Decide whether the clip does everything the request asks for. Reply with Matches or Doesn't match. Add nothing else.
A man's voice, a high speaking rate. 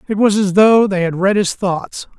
Matches